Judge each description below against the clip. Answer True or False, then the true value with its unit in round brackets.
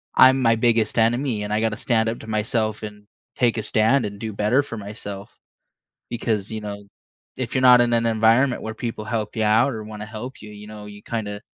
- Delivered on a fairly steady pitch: True (1.9 semitones)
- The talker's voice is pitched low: True (110 Hz)